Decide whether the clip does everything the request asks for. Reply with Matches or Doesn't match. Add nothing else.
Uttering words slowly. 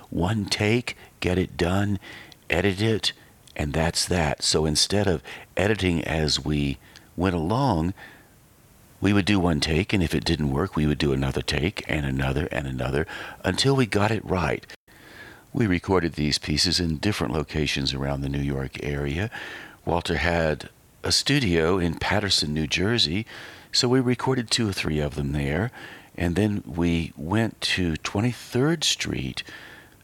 Doesn't match